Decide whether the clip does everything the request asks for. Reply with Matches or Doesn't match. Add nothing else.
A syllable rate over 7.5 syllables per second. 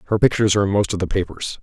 Matches